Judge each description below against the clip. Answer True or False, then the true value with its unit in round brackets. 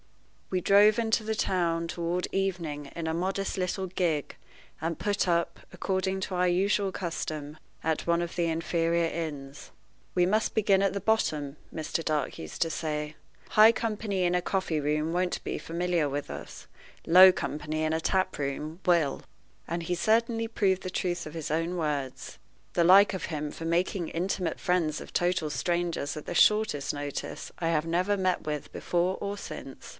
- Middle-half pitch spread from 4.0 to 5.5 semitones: False (3.3 semitones)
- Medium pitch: True (175 Hz)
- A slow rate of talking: False (175 wpm)